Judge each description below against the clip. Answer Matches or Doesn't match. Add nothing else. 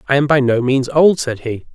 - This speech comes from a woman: Doesn't match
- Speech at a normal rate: Doesn't match